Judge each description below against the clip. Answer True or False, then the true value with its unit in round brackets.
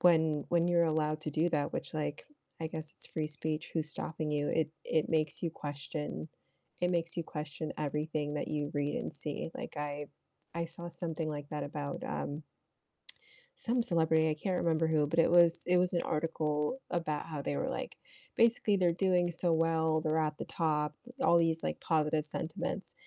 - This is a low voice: False (160 Hz)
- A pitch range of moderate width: False (2.0 semitones)